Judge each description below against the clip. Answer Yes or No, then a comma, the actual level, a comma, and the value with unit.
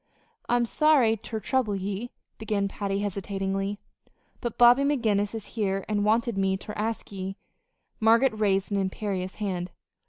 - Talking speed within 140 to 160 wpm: Yes, average, 150 wpm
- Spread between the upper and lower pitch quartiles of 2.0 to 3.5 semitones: Yes, average, 2.7 semitones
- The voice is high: Yes, high, 205 Hz